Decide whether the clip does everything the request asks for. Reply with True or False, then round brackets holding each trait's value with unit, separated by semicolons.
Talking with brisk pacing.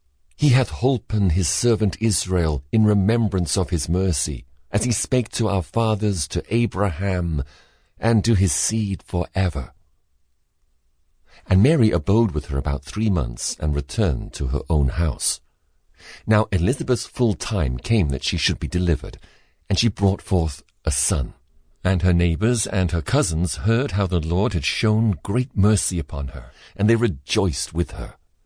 False (160 wpm)